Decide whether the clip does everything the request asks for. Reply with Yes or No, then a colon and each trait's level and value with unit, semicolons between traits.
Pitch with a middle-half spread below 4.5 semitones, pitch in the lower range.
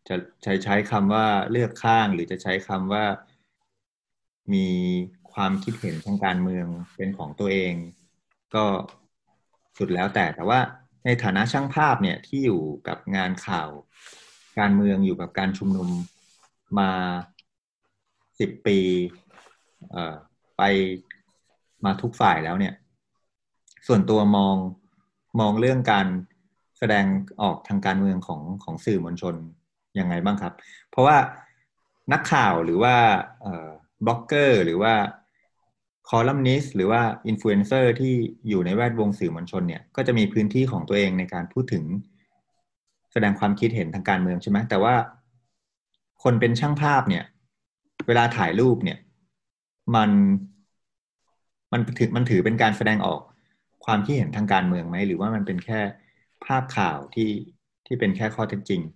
Yes: average, 4.0 semitones; low, 100 Hz